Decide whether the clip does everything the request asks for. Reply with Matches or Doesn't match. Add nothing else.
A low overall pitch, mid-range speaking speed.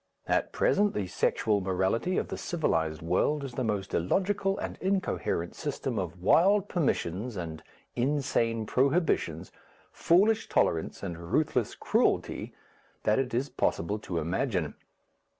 Doesn't match